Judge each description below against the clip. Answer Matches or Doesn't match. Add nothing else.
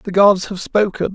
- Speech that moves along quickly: Matches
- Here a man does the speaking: Matches